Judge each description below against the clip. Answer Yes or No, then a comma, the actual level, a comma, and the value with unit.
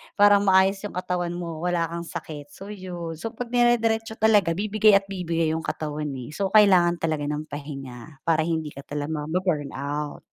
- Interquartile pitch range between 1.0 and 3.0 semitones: No, average, 4.5 semitones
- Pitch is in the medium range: Yes, medium, 170 Hz